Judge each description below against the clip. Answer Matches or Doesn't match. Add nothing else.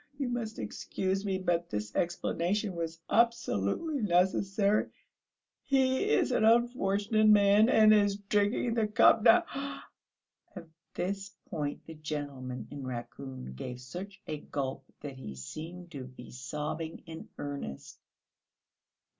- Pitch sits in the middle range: Matches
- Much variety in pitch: Matches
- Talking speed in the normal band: Doesn't match